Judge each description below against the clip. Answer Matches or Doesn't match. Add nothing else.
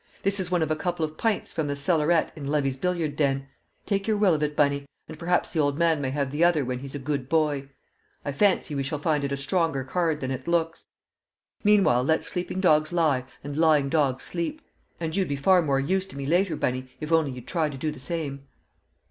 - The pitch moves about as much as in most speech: Matches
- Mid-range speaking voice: Matches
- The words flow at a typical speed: Doesn't match